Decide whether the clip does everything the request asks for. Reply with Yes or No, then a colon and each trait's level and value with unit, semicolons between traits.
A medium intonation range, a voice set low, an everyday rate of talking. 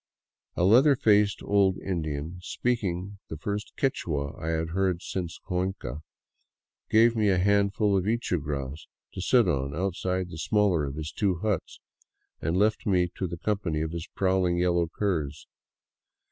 Yes: average, 3.9 semitones; very low, 90 Hz; average, 160 wpm